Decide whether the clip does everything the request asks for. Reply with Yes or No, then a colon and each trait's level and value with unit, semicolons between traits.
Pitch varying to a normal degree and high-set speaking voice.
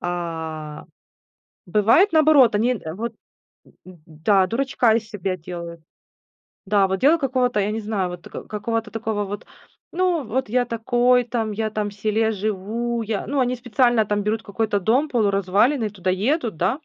Yes: average, 3.8 semitones; high, 215 Hz